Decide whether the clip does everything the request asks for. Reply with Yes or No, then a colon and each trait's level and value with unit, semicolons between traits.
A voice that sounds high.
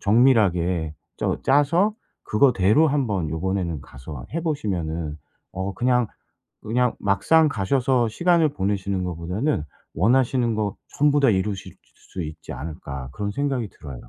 No: low, 100 Hz